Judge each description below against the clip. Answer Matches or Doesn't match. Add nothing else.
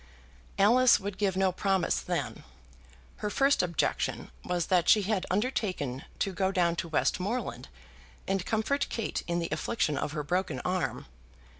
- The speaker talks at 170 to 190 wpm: Doesn't match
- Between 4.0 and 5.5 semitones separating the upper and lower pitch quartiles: Doesn't match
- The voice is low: Doesn't match